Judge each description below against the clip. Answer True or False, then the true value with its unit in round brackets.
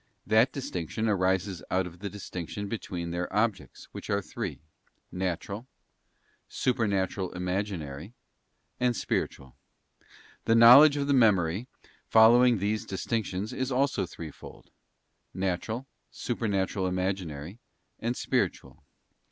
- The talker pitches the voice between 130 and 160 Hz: False (100 Hz)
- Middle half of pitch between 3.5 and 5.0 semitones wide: True (4.0 semitones)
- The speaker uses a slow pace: True (105 wpm)